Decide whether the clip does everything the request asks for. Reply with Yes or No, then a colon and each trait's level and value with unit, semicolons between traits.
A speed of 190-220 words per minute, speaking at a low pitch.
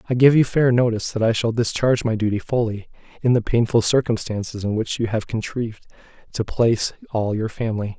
Yes: average, 195 wpm; low, 115 Hz